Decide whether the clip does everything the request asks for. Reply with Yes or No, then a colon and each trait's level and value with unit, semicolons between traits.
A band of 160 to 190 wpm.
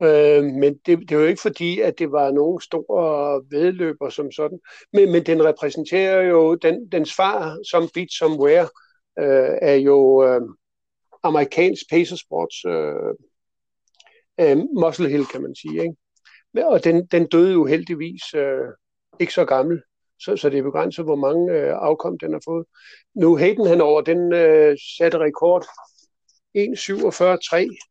No: average, 150 wpm